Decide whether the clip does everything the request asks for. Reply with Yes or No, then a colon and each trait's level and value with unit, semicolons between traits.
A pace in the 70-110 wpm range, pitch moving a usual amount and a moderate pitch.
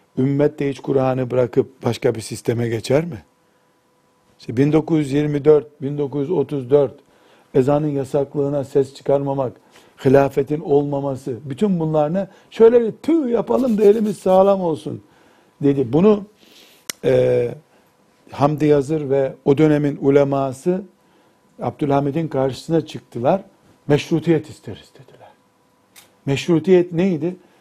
Yes: average, 100 wpm; average, 3.4 semitones; medium, 145 Hz